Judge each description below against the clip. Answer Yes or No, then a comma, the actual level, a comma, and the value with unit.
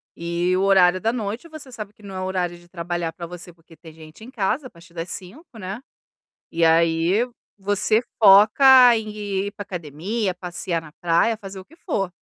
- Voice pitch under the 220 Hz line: Yes, medium, 185 Hz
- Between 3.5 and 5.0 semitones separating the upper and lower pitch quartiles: Yes, average, 4.0 semitones